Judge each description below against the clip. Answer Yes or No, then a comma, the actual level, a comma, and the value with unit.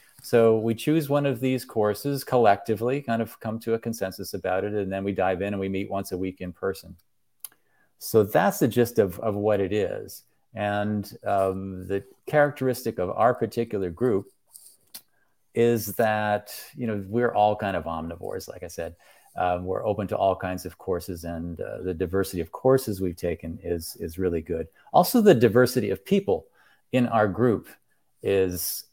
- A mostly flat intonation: No, average, 4.3 semitones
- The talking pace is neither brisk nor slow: Yes, average, 180 wpm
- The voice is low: Yes, low, 105 Hz